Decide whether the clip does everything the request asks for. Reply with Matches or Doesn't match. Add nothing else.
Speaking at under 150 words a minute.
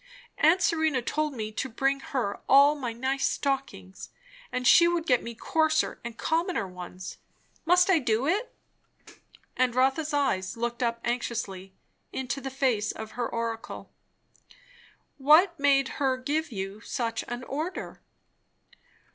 Matches